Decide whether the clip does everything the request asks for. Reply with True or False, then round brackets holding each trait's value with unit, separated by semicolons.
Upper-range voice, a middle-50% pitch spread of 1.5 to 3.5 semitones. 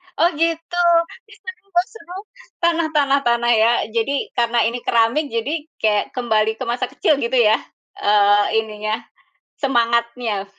False (235 Hz; 5.0 semitones)